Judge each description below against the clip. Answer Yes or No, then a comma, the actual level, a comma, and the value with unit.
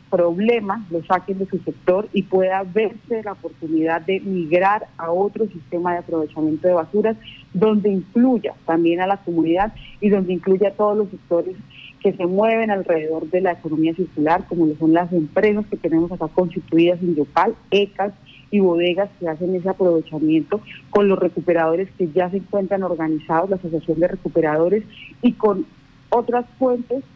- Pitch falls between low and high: Yes, medium, 180 Hz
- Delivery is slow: No, average, 165 wpm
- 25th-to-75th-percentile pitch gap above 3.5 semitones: No, average, 3.2 semitones